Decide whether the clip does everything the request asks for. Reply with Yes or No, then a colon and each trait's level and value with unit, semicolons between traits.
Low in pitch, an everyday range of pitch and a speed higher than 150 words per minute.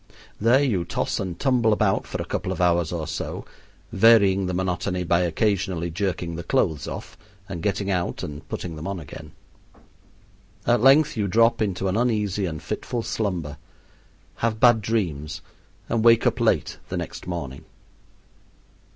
Yes: very low, 95 Hz; average, 4.7 semitones; average, 160 wpm